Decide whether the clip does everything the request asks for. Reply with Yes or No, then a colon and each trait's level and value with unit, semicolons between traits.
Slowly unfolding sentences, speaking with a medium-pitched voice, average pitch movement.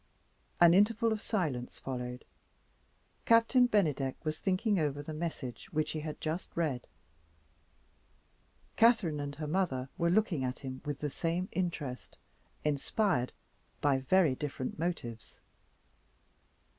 No: slow, 120 wpm; medium, 155 Hz; wide, 5.7 semitones